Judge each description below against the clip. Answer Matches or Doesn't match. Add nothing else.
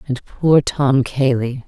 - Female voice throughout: Matches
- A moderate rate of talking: Matches